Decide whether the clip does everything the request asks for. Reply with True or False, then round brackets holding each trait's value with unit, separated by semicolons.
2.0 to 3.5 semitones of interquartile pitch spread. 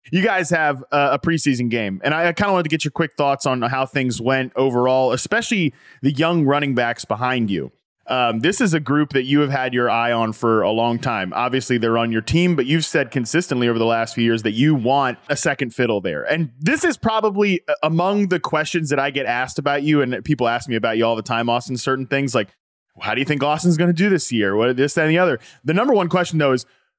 False (5.2 semitones)